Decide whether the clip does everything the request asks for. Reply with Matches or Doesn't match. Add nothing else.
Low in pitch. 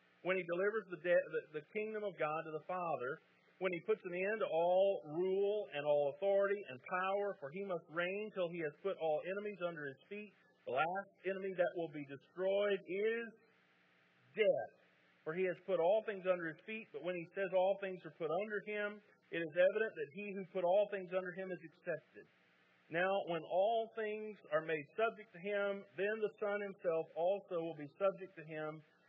Doesn't match